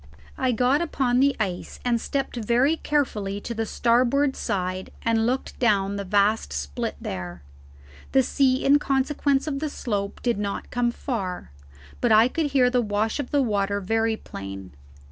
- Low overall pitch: No, high, 235 Hz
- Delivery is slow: No, average, 170 wpm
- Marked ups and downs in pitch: No, average, 4.9 semitones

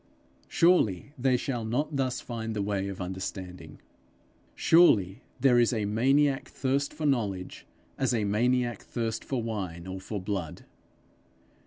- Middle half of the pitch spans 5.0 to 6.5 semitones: Yes, average, 5.3 semitones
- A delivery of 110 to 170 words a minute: Yes, average, 140 wpm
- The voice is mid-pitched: No, low, 115 Hz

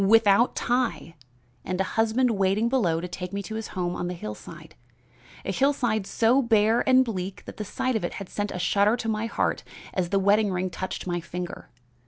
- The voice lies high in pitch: Yes, high, 205 Hz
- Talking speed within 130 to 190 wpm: No, fast, 205 wpm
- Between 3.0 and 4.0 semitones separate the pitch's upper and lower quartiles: Yes, average, 3.7 semitones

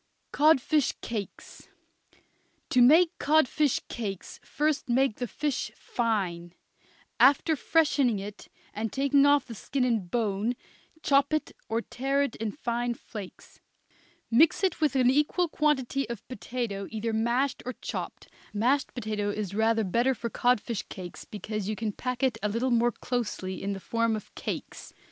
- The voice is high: Yes, high, 240 Hz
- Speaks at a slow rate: No, average, 150 wpm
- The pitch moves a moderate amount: Yes, average, 4.3 semitones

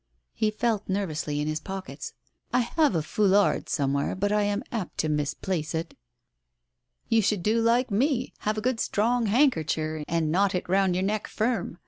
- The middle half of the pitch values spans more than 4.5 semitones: Yes, wide, 5.4 semitones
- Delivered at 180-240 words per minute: Yes, average, 185 wpm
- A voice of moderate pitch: No, high, 200 Hz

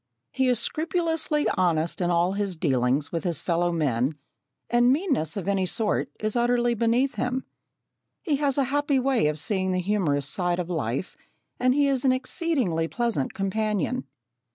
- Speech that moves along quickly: No, average, 165 wpm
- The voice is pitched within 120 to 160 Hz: No, high, 205 Hz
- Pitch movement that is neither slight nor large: No, wide, 7.2 semitones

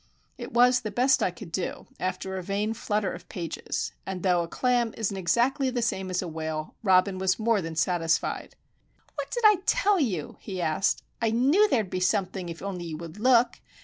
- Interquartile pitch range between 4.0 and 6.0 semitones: Yes, average, 5.0 semitones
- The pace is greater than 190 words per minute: Yes, average, 200 wpm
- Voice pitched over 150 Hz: Yes, high, 190 Hz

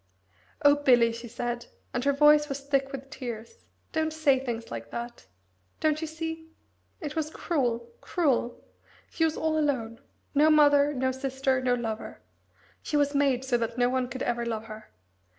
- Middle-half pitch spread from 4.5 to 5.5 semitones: No, average, 3.8 semitones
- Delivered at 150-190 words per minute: Yes, average, 170 wpm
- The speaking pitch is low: No, very high, 265 Hz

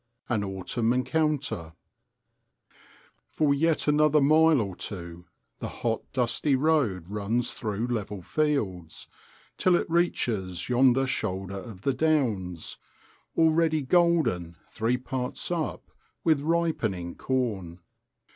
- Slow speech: Yes, slow, 110 wpm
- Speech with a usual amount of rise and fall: No, wide, 7.8 semitones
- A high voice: No, low, 125 Hz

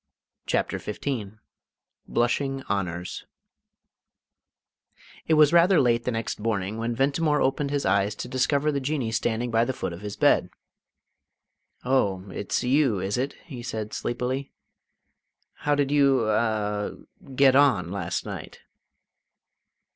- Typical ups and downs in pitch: Yes, average, 5.0 semitones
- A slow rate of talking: Yes, slow, 130 wpm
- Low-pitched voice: Yes, low, 120 Hz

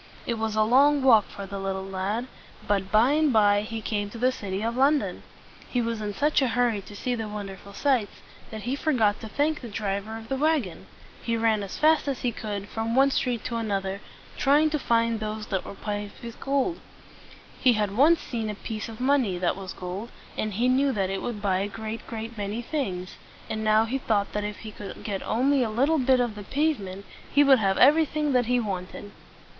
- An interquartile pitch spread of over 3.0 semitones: Yes, average, 4.0 semitones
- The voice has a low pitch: No, high, 225 Hz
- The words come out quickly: Yes, fast, 220 wpm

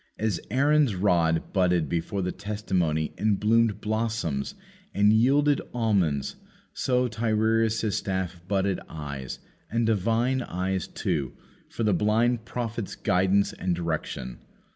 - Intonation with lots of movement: No, average, 4.2 semitones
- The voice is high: No, low, 105 Hz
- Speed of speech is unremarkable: No, slow, 120 wpm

